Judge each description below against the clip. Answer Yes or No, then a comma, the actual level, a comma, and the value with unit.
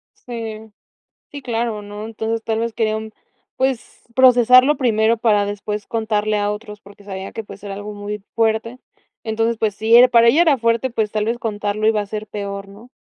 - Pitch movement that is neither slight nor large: No, narrow, 1.9 semitones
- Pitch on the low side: No, high, 220 Hz